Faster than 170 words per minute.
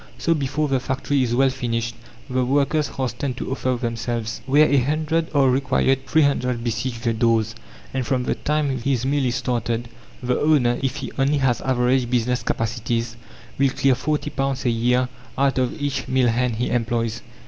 Yes: average, 180 wpm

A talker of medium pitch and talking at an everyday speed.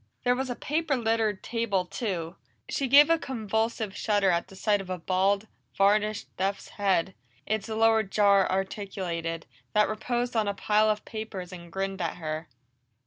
No: high, 205 Hz; average, 165 wpm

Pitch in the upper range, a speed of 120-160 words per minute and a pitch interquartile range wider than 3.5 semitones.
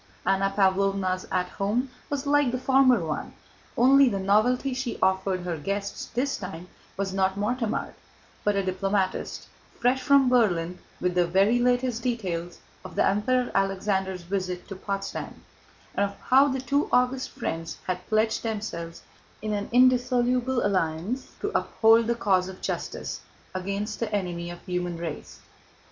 Yes: high, 200 Hz; average, 155 wpm; average, 5.0 semitones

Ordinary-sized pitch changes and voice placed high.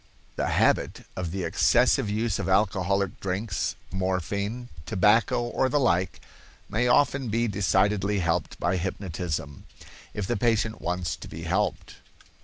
No: average, 3.4 semitones; low, 100 Hz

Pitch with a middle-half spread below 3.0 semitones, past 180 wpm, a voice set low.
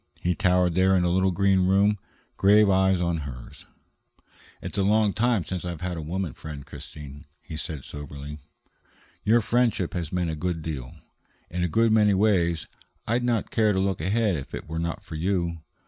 No: average, 3.6 semitones; average, 190 wpm; very low, 90 Hz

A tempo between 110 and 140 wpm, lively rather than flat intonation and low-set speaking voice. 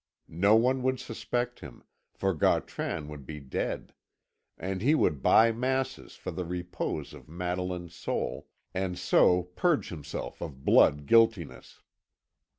Yes: slow, 135 wpm; wide, 6.3 semitones; very low, 90 Hz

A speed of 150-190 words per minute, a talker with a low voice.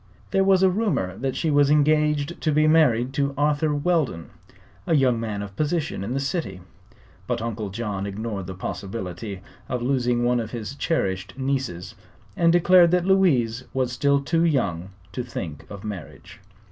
Yes: average, 170 wpm; low, 130 Hz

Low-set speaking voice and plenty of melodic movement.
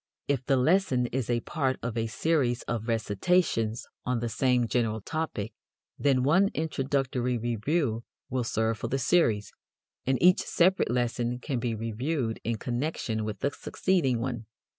No: low, 125 Hz; average, 3.7 semitones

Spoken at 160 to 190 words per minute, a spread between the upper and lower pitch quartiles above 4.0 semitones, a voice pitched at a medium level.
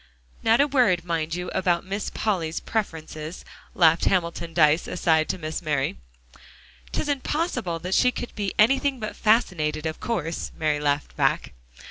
No: average, 150 wpm; wide, 5.5 semitones; medium, 175 Hz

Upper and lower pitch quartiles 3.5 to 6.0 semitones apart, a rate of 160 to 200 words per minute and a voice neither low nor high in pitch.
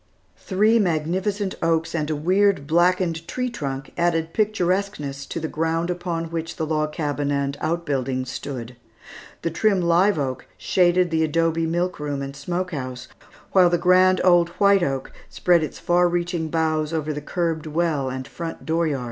No: average, 3.1 semitones; average, 165 wpm; medium, 165 Hz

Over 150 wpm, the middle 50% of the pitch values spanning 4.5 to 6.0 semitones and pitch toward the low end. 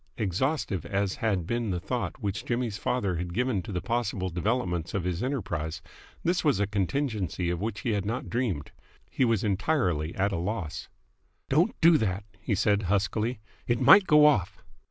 Yes: average, 175 wpm; average, 4.9 semitones; low, 105 Hz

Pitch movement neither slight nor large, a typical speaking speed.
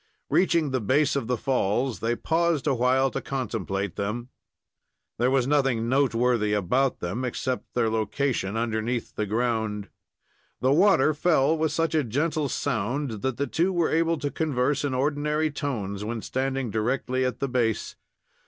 Yes: average, 4.1 semitones; average, 160 wpm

